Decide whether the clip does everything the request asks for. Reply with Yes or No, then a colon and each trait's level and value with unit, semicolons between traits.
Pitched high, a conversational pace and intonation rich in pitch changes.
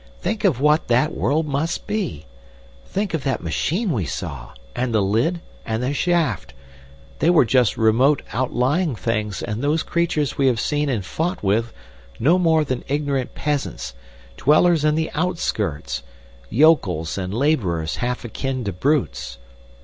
No: low, 135 Hz; average, 150 wpm; wide, 6.2 semitones